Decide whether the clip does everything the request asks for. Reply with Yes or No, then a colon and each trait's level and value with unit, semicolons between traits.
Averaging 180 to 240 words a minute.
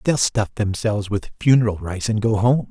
Yes: average, 200 wpm